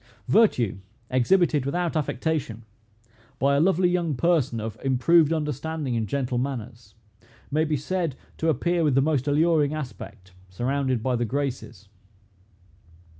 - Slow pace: Yes, slow, 130 wpm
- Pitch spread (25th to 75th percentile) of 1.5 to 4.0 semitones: No, average, 4.5 semitones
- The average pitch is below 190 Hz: Yes, medium, 140 Hz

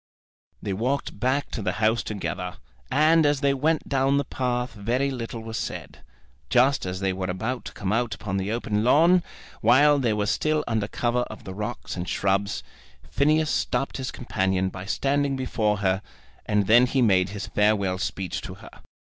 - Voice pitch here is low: Yes, low, 115 Hz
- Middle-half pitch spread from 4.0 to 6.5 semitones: Yes, average, 5.2 semitones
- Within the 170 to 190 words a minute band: Yes, average, 180 wpm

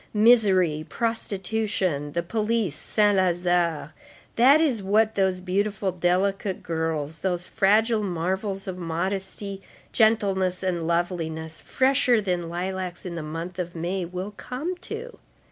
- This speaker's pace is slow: Yes, slow, 120 wpm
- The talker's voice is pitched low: No, medium, 185 Hz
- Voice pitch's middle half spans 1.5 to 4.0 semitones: Yes, average, 3.5 semitones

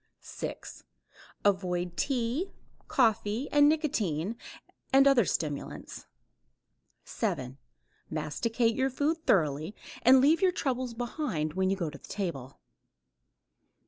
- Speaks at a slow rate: Yes, slow, 110 wpm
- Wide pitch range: Yes, wide, 8.2 semitones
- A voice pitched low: No, high, 225 Hz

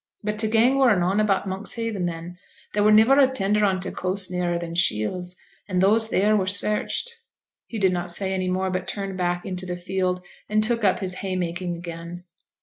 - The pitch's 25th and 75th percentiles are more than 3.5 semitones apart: No, average, 2.9 semitones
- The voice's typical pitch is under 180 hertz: No, high, 190 Hz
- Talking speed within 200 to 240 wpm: Yes, fast, 205 wpm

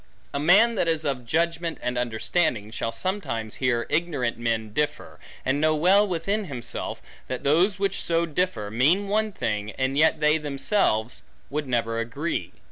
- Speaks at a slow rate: No, average, 160 wpm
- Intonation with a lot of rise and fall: Yes, wide, 6.7 semitones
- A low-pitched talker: No, medium, 150 Hz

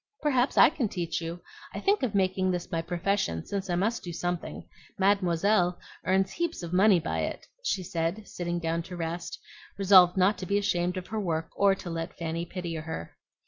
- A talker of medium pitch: Yes, medium, 180 Hz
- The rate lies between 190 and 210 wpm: Yes, average, 195 wpm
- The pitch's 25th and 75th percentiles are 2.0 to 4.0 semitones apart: Yes, average, 2.8 semitones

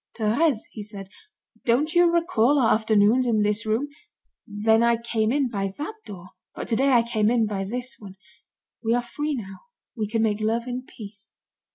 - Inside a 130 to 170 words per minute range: No, average, 185 wpm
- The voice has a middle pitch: No, high, 225 Hz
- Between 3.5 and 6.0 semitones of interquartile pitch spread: No, average, 3.0 semitones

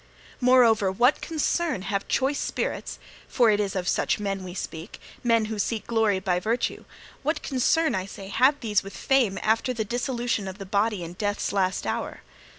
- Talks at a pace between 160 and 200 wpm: Yes, average, 180 wpm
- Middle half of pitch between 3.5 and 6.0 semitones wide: Yes, average, 4.0 semitones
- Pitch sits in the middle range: No, high, 215 Hz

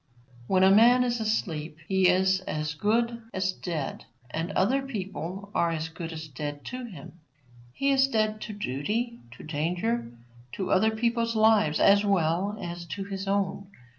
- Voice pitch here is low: No, high, 190 Hz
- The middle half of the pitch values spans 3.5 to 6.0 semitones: Yes, average, 5.1 semitones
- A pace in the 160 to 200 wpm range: Yes, average, 165 wpm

